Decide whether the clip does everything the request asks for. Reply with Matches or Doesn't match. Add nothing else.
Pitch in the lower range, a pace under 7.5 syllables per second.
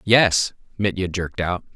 Matches